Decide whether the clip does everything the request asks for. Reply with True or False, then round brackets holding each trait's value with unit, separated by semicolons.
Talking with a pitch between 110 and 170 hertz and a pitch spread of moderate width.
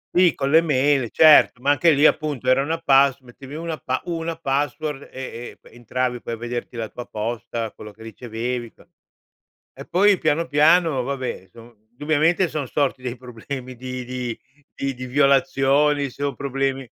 True (135 Hz; 3.3 semitones)